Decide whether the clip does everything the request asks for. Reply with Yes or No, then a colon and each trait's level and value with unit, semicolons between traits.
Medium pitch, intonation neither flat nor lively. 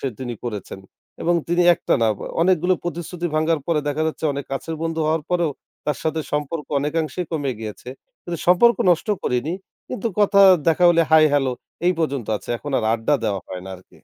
Yes: medium, 155 Hz; average, 4.0 semitones